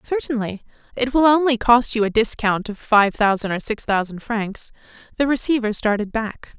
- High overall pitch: Yes, high, 225 Hz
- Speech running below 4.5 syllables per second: No, 5.0 syllables/s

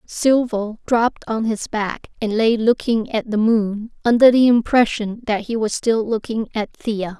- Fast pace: No, average, 175 wpm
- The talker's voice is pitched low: No, high, 225 Hz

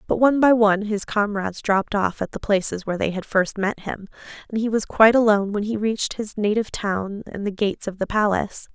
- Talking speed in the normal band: No, fast, 235 wpm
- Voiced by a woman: Yes, female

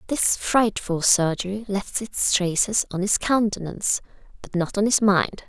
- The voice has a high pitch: Yes, high, 200 Hz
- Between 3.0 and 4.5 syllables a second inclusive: Yes, 4.4 syllables/s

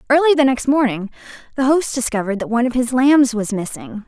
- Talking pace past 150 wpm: Yes, fast, 205 wpm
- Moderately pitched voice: No, very high, 250 Hz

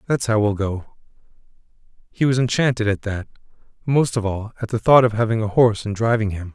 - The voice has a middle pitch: No, low, 110 Hz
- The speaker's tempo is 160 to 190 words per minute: No, average, 200 wpm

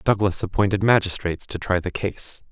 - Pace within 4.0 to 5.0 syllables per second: No, 5.5 syllables/s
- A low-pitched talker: Yes, very low, 95 Hz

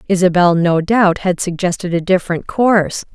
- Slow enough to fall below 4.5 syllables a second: No, 5.1 syllables/s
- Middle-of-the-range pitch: Yes, medium, 180 Hz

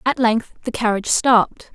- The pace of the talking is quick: No, average, 170 wpm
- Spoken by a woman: Yes, female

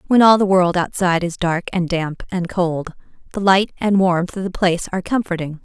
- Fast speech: Yes, fast, 215 wpm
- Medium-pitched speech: Yes, medium, 180 Hz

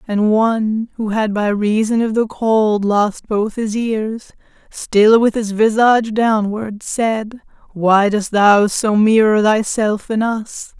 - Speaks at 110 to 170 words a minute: Yes, average, 150 wpm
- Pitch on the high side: Yes, high, 215 Hz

